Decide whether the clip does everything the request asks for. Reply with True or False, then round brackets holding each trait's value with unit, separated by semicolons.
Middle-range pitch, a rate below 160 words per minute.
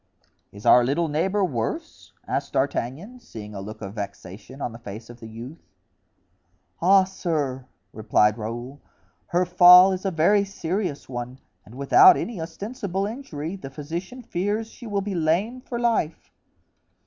True (165 Hz; 150 wpm)